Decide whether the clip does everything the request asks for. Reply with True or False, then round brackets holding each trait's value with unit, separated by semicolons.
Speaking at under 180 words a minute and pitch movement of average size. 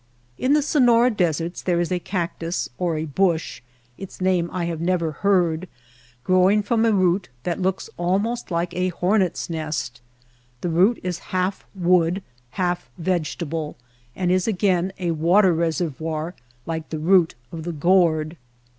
False (150 wpm; 2.3 semitones)